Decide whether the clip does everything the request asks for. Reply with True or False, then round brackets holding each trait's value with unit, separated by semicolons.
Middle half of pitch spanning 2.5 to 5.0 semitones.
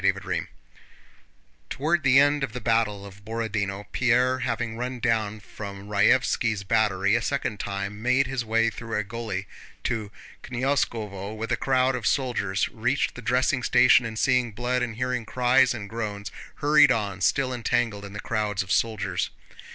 True (3.6 semitones)